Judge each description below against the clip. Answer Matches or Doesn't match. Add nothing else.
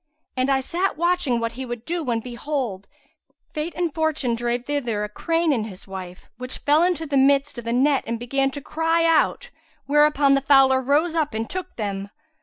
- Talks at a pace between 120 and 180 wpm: Doesn't match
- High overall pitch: Matches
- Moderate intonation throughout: Matches